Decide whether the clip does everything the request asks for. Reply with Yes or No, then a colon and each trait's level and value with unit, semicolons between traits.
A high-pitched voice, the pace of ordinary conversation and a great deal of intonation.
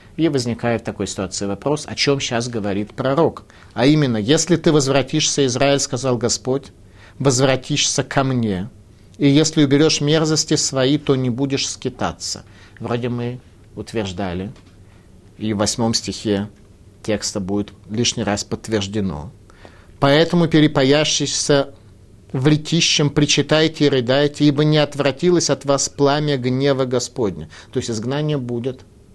No: low, 125 Hz; average, 130 wpm; wide, 5.7 semitones